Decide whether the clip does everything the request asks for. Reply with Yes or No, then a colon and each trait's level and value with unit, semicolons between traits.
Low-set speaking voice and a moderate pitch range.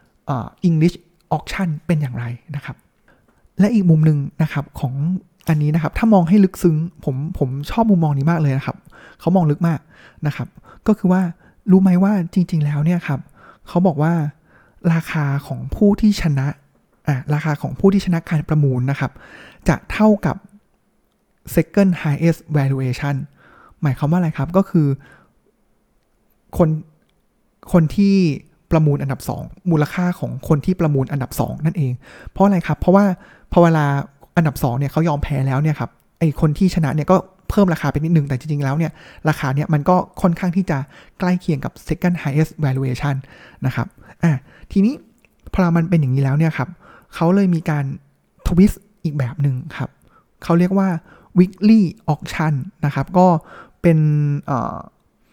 No: medium, 160 Hz; average, 3.9 semitones